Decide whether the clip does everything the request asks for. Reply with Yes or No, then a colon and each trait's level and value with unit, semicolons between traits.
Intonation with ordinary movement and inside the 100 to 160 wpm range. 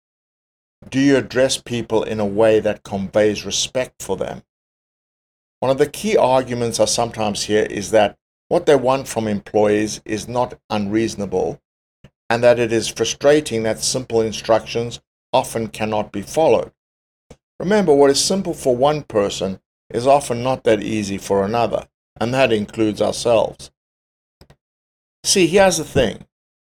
Yes: average, 4.0 semitones; average, 145 wpm